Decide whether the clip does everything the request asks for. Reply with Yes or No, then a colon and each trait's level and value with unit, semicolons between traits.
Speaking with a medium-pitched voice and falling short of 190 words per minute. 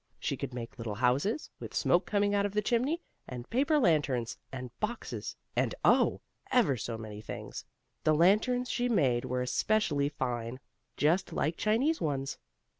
Yes: medium, 155 Hz; average, 160 wpm